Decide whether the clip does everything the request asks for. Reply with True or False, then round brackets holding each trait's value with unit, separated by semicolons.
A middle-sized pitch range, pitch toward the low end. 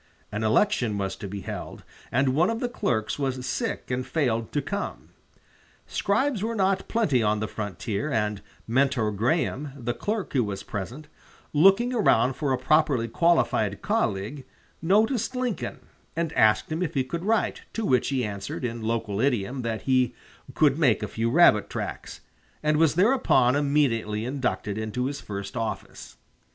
False (7.0 semitones; 130 Hz)